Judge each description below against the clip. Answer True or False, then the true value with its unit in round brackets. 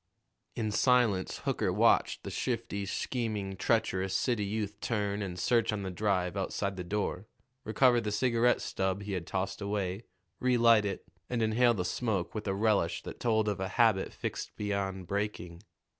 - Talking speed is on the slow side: False (165 wpm)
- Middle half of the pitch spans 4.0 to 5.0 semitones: False (2.7 semitones)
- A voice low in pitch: True (105 Hz)